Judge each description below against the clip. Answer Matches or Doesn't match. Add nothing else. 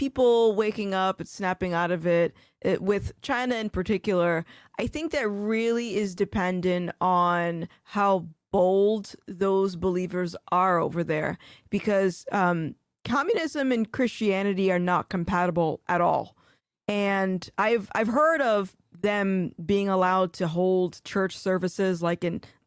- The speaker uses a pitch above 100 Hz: Matches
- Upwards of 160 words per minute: Doesn't match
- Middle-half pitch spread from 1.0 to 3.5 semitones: Matches